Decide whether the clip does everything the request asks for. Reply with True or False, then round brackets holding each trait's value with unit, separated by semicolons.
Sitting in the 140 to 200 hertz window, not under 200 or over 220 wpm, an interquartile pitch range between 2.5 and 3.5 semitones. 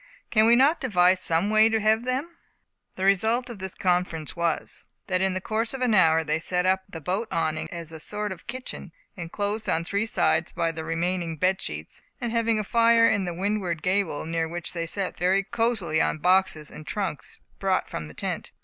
False (190 Hz; 205 wpm; 4.7 semitones)